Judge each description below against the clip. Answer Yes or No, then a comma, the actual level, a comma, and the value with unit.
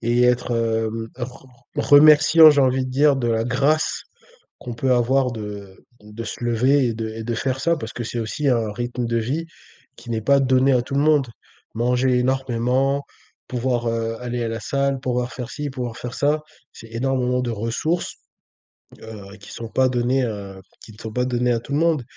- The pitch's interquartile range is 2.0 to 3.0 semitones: Yes, average, 2.7 semitones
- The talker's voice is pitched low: Yes, low, 125 Hz